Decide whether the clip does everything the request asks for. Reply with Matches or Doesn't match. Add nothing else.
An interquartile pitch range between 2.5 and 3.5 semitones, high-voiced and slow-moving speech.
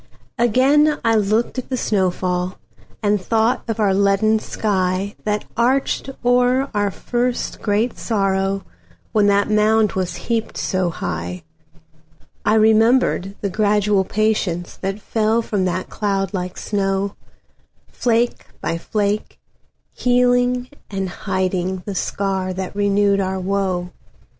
Matches